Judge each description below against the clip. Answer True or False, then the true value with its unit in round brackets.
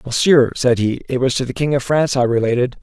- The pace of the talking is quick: True (255 wpm)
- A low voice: True (130 Hz)